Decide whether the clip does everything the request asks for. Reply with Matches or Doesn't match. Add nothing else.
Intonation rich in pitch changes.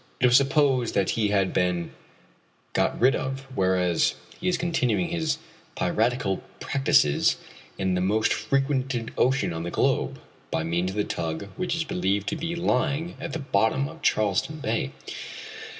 Matches